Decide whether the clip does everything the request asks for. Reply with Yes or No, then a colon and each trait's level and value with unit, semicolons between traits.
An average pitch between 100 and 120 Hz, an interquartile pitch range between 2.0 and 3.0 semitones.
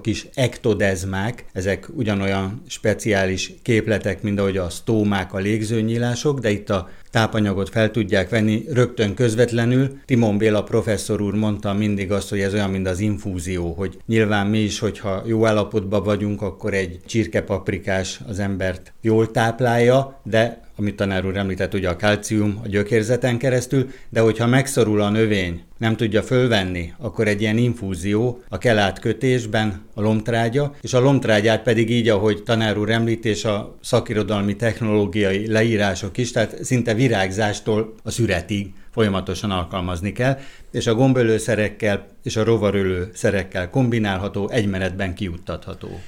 Yes: low, 105 Hz; average, 2.7 semitones